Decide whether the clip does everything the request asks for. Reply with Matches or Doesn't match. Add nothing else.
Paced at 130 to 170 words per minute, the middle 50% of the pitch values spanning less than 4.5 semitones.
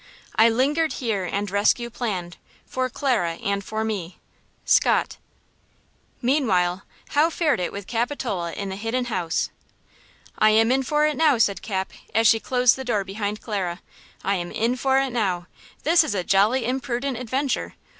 Doesn't match